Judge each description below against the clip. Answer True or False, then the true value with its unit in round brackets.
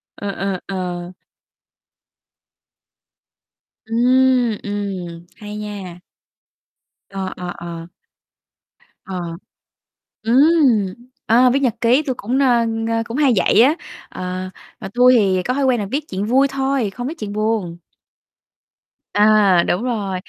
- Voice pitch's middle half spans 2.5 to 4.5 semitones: False (5.0 semitones)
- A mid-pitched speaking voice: False (215 Hz)